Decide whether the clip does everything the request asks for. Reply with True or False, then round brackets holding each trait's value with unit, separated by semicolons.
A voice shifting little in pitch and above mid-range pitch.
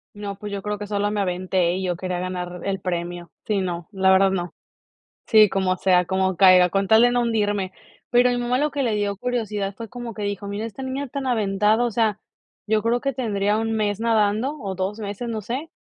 False (3.3 semitones; 205 Hz)